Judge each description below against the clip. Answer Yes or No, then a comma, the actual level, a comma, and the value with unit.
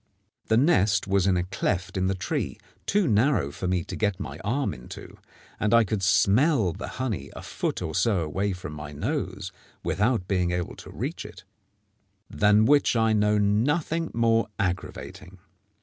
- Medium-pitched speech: No, low, 100 Hz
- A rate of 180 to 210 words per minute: No, average, 170 wpm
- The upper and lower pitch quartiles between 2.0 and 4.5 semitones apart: Yes, average, 3.8 semitones